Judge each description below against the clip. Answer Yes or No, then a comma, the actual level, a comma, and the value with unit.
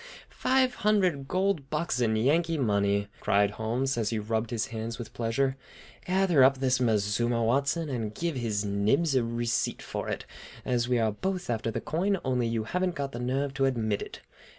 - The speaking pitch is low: Yes, low, 125 Hz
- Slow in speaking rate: No, average, 190 wpm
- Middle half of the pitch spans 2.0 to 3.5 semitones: No, average, 4.8 semitones